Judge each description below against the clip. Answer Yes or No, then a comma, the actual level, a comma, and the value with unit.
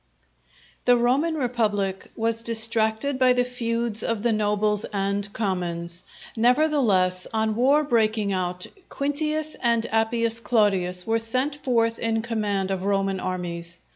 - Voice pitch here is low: No, high, 225 Hz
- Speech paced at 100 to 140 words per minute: Yes, slow, 135 wpm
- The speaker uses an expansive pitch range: No, average, 3.5 semitones